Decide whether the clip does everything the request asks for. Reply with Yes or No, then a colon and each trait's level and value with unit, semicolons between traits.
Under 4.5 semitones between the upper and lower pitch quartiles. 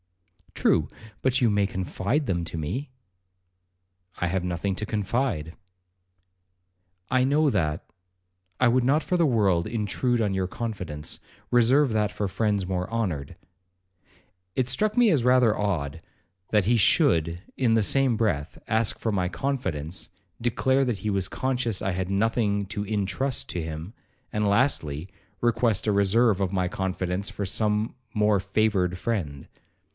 No: average, 4.8 semitones